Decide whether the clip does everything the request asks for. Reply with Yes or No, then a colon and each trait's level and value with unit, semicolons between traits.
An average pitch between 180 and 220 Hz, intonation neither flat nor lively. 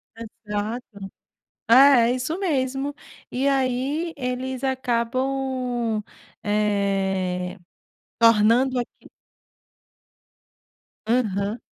No: high, 245 Hz; average, 3.8 semitones